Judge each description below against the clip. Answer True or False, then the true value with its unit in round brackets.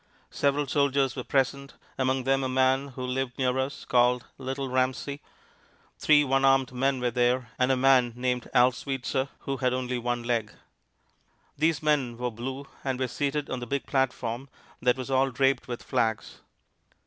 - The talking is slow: False (170 wpm)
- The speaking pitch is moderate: False (130 Hz)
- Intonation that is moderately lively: False (1.5 semitones)